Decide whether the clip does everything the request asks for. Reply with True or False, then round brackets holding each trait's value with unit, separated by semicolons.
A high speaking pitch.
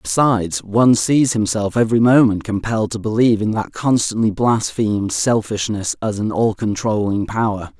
False (110 Hz)